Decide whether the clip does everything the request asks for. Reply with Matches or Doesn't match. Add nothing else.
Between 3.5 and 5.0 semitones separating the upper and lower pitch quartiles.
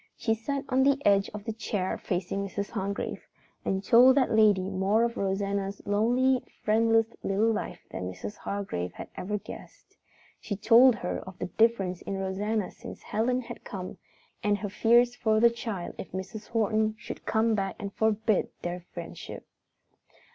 Doesn't match